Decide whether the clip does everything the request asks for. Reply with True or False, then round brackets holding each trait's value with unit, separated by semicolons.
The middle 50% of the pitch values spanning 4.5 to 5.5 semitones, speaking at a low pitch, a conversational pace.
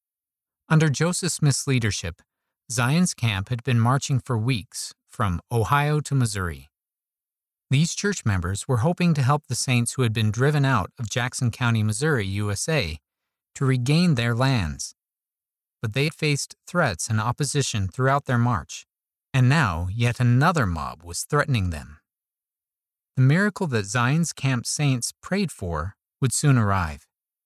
True (5.1 semitones; 125 Hz; 145 wpm)